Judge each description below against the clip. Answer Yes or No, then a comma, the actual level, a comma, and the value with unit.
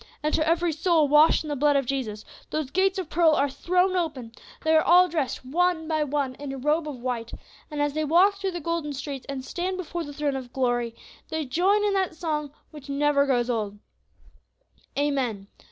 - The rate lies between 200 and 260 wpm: Yes, fast, 205 wpm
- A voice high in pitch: Yes, very high, 300 Hz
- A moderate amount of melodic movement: Yes, average, 3.9 semitones